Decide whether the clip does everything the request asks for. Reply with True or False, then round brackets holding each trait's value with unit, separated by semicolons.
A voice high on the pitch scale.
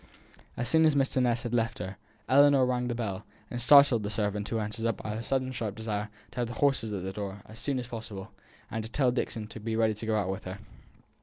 False (115 Hz)